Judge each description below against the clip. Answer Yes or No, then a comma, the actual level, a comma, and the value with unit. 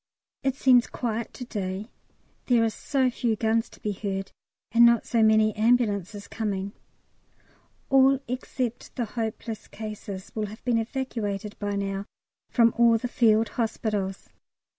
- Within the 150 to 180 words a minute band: No, average, 140 wpm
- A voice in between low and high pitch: No, high, 220 Hz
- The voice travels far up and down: No, average, 2.7 semitones